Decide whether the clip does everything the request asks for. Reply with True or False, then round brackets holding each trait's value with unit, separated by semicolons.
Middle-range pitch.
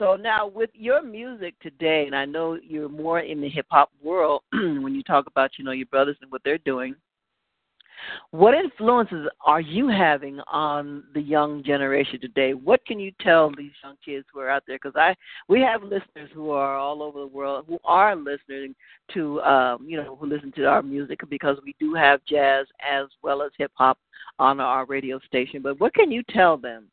True (145 Hz)